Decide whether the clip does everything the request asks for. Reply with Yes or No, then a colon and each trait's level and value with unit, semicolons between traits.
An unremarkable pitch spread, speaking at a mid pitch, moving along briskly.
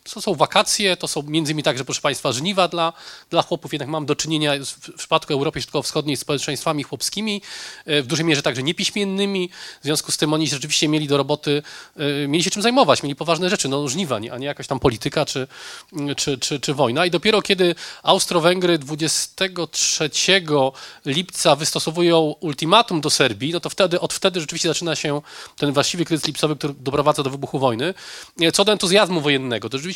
Yes: average, 3.3 semitones; medium, 155 Hz; fast, 185 wpm